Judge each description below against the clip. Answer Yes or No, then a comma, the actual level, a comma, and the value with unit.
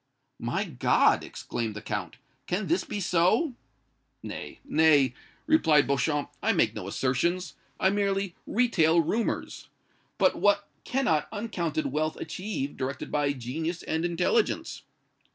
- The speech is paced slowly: Yes, slow, 125 wpm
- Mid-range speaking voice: Yes, medium, 170 Hz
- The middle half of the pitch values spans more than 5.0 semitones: Yes, wide, 5.6 semitones